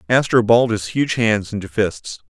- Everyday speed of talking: Yes, average, 180 wpm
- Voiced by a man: Yes, male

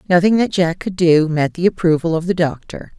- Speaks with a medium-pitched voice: Yes, medium, 170 Hz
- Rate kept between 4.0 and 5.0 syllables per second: No, 5.4 syllables/s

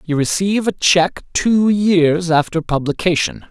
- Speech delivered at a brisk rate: No, slow, 135 wpm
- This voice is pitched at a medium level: Yes, medium, 170 Hz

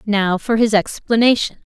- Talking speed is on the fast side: No, average, 140 wpm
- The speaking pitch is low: No, high, 215 Hz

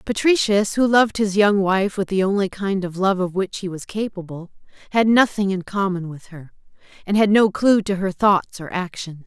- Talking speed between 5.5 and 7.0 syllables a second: No, 5.0 syllables/s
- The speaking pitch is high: Yes, high, 195 Hz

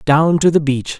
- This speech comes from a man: Yes, male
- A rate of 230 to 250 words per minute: Yes, fast, 240 wpm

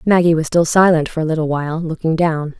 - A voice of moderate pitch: Yes, medium, 160 Hz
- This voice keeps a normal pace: No, fast, 230 wpm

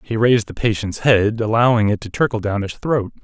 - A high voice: No, low, 110 Hz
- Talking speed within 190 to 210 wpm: No, fast, 225 wpm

